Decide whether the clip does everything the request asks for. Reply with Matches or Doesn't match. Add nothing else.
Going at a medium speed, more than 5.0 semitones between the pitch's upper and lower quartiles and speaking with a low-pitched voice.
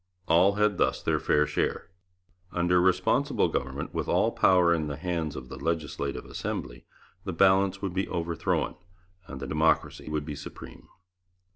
Doesn't match